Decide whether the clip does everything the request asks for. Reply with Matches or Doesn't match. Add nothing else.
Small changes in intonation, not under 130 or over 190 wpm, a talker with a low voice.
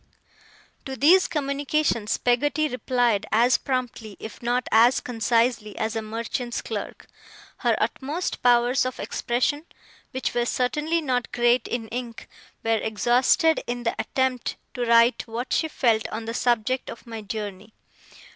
Doesn't match